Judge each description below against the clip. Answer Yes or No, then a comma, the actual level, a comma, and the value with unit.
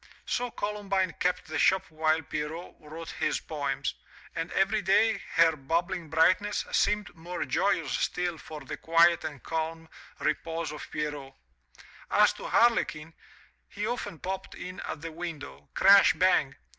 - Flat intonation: No, average, 3.4 semitones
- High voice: No, medium, 165 Hz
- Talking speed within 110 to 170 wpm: Yes, average, 145 wpm